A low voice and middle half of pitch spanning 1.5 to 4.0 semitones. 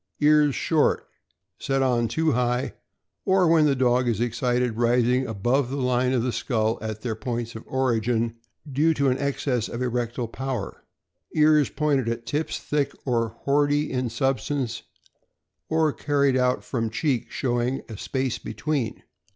Yes: low, 125 Hz; average, 3.1 semitones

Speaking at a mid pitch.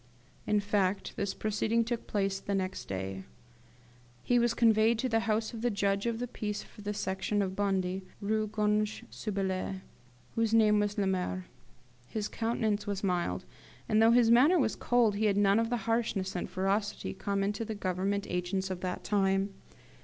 No: high, 205 Hz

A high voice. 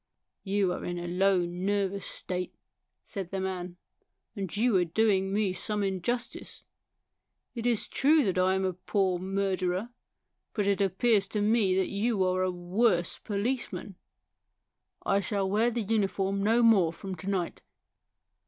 Yes: high, 195 Hz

